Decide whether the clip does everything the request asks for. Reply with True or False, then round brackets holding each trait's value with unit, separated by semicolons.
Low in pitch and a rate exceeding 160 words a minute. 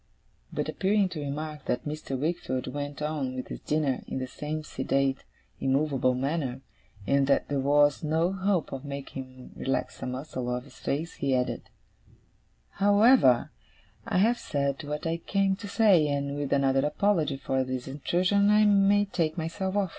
False (145 Hz; 170 wpm)